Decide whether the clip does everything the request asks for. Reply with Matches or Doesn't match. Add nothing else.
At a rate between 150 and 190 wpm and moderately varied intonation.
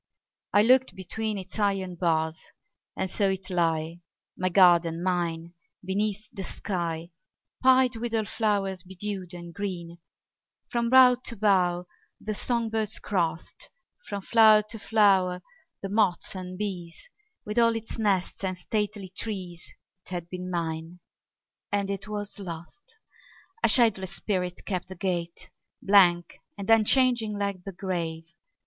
Doesn't match